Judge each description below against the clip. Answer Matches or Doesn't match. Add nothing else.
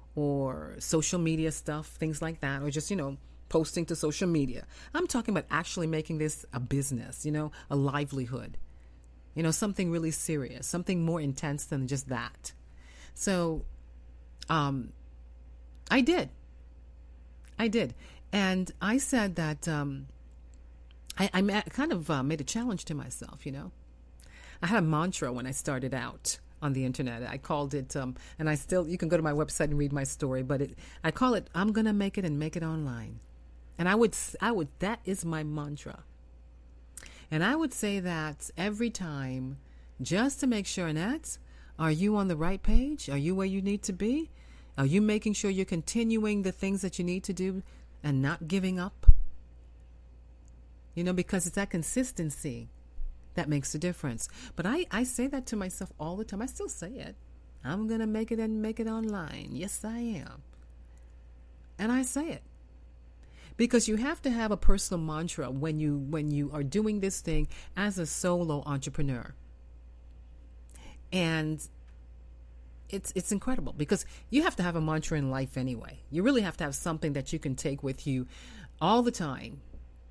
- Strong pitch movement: Matches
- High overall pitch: Doesn't match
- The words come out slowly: Doesn't match